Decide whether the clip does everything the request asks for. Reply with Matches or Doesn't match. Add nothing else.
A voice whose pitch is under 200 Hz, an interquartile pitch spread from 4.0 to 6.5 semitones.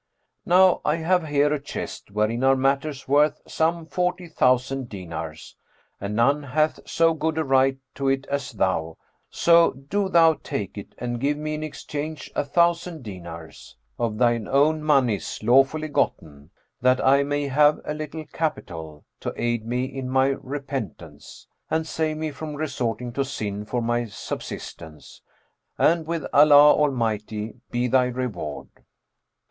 Matches